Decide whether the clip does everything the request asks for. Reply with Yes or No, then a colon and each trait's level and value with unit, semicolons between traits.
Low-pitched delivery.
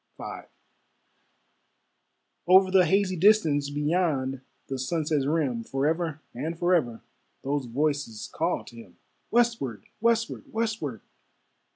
No: medium, 155 Hz